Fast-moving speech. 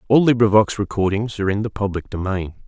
No: average, 180 wpm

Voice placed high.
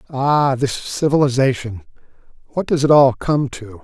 No: low, 135 Hz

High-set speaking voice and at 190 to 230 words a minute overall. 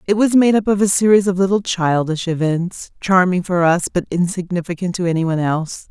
No: medium, 180 Hz; fast, 205 wpm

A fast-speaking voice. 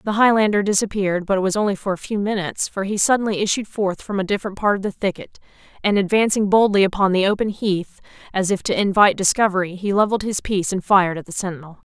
Yes: fast, 220 wpm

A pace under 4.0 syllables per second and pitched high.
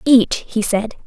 Yes: 3.7 syllables/s; high, 225 Hz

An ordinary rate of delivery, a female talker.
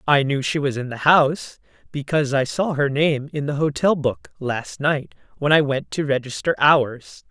Yes: average, 195 wpm; female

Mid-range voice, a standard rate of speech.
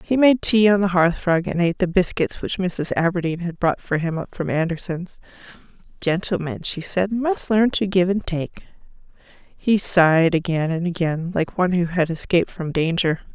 Yes: medium, 180 Hz; average, 190 wpm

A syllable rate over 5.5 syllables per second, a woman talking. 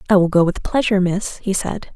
Yes: 6.0 syllables/s; female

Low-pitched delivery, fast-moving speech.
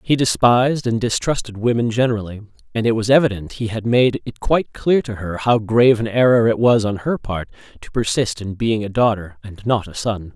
Yes: low, 110 Hz; fast, 215 wpm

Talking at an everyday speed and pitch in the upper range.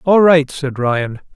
No: average, 175 wpm; medium, 145 Hz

